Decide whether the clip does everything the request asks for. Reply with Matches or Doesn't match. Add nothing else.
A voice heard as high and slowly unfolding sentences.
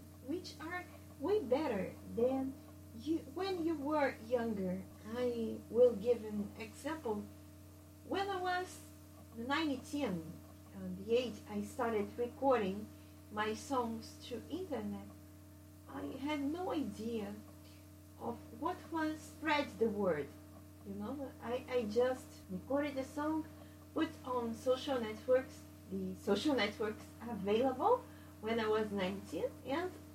Matches